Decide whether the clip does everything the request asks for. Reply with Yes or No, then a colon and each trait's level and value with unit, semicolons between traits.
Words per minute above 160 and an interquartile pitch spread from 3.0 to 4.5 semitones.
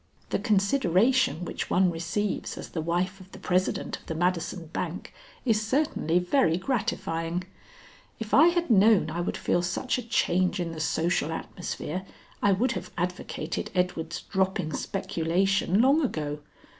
No: average, 150 wpm; average, 3.9 semitones